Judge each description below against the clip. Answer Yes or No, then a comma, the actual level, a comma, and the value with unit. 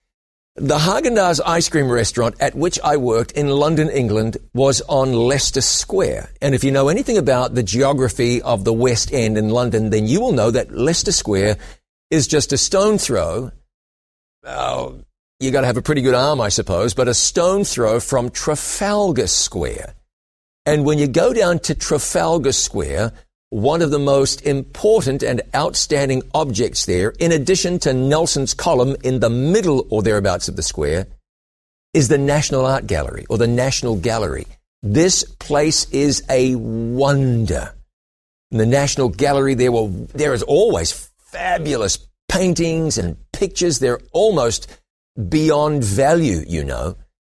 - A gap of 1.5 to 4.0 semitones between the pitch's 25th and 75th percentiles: No, average, 4.9 semitones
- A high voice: No, low, 130 Hz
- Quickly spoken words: No, average, 155 wpm